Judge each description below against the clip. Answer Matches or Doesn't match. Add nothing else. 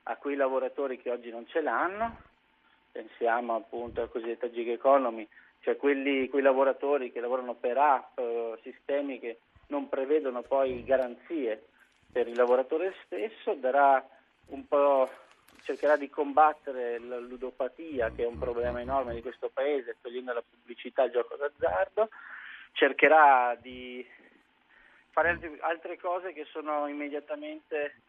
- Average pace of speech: Matches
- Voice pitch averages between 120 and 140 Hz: Matches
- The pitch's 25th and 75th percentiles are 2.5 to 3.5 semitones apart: Doesn't match